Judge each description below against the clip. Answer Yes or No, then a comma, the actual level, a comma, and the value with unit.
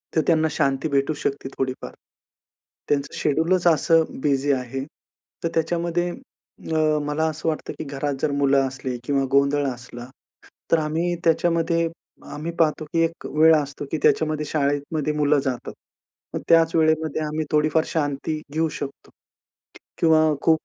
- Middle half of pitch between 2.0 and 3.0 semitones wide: Yes, narrow, 2.4 semitones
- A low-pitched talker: No, medium, 155 Hz